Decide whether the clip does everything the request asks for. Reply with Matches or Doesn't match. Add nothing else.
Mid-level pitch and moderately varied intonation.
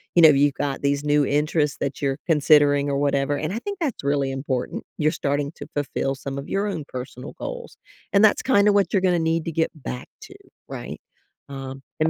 Matches